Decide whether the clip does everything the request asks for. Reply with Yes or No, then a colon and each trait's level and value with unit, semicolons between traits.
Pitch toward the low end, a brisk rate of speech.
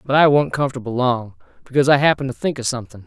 Yes: low, 130 Hz; fast, 235 wpm